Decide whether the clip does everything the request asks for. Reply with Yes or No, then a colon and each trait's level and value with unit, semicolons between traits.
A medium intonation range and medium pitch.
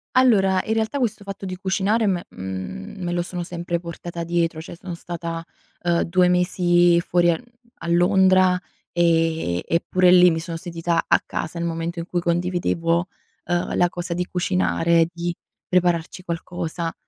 No: narrow, 1.4 semitones; medium, 175 Hz